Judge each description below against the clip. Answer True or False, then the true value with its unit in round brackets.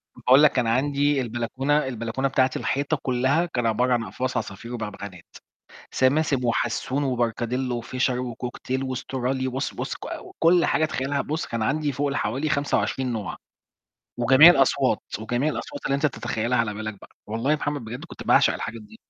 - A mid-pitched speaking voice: False (130 Hz)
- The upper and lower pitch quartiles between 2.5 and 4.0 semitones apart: True (3.2 semitones)